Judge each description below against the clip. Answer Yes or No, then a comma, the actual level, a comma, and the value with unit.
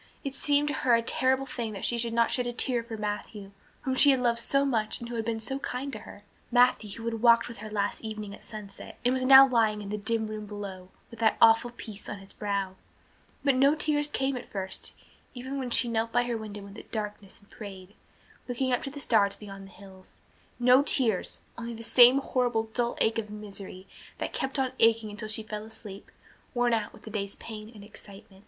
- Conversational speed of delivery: No, fast, 230 wpm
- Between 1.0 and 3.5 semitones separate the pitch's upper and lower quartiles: Yes, average, 2.9 semitones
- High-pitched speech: Yes, high, 225 Hz